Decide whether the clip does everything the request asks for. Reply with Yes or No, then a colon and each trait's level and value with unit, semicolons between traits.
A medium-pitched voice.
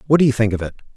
No: low, 120 Hz